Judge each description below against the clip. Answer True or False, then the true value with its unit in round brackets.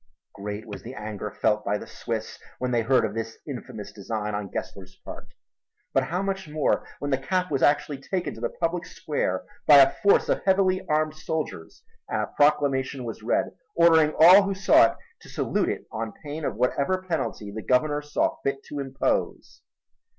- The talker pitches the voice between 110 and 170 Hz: True (140 Hz)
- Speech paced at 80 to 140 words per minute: False (185 wpm)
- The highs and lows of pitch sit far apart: True (6.3 semitones)